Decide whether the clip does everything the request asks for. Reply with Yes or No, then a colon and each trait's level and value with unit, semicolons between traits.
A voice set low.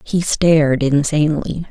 No: medium, 150 Hz